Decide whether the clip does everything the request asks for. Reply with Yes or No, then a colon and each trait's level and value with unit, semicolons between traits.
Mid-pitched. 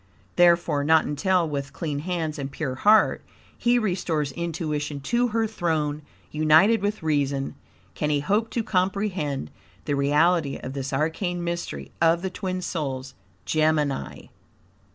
Yes: medium, 160 Hz